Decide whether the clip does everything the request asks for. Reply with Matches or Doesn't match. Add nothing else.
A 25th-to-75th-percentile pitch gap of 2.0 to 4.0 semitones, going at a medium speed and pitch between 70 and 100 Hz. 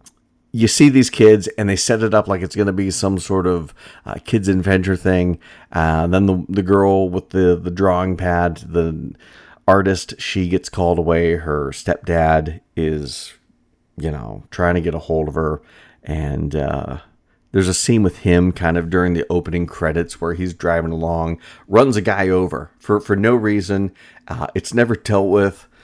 Matches